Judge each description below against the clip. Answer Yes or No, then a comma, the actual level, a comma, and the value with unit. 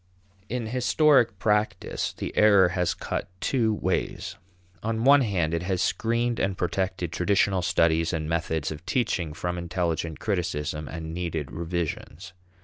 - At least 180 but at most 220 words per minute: No, average, 140 wpm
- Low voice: Yes, very low, 90 Hz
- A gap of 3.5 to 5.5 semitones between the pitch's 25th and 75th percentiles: Yes, average, 4.4 semitones